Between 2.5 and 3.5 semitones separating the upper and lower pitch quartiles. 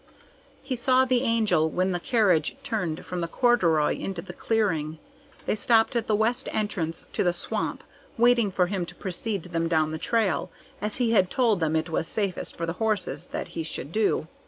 No: average, 5.2 semitones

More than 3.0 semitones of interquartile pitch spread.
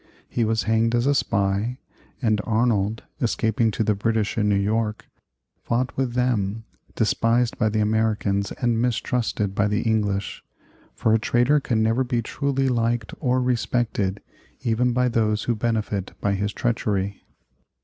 No: narrow, 2.4 semitones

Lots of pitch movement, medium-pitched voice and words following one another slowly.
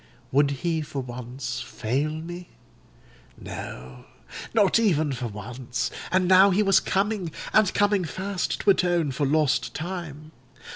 Yes: wide, 6.3 semitones; medium, 155 Hz; slow, 115 wpm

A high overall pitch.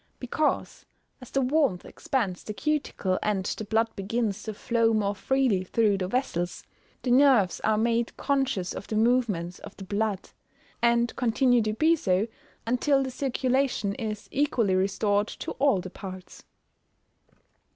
Yes: high, 225 Hz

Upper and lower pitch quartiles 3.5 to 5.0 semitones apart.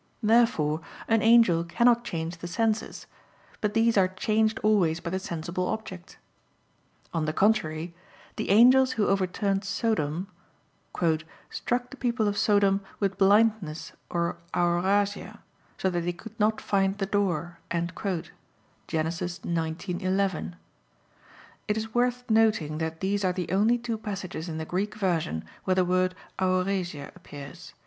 Yes: average, 4.0 semitones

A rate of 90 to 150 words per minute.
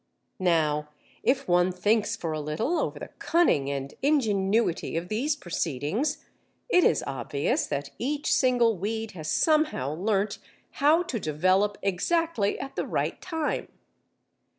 Yes: slow, 135 wpm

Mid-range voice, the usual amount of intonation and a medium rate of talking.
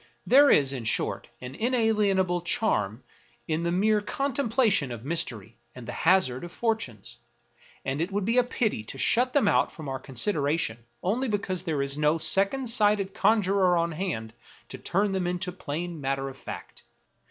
No: medium, 175 Hz; wide, 7.3 semitones; average, 170 wpm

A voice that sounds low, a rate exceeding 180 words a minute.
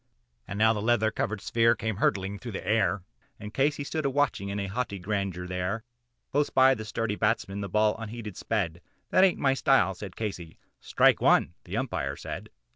Yes: low, 105 Hz; average, 195 wpm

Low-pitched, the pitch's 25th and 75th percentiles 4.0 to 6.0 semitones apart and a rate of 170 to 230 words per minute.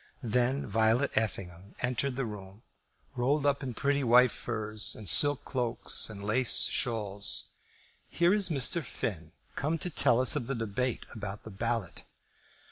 No: low, 120 Hz; average, 4.4 semitones; average, 150 wpm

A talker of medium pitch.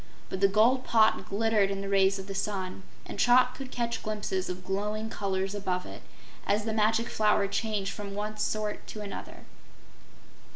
No: high, 210 Hz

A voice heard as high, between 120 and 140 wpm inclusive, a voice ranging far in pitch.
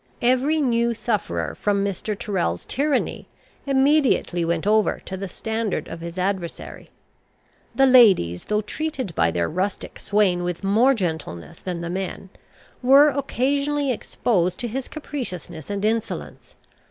Yes: high, 210 Hz; slow, 135 wpm; wide, 6.4 semitones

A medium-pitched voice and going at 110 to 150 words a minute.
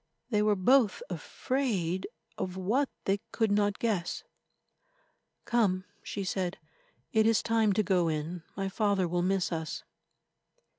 No: high, 195 Hz; slow, 135 wpm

